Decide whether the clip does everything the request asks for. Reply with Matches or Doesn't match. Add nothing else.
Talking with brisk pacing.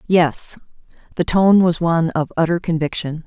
Doesn't match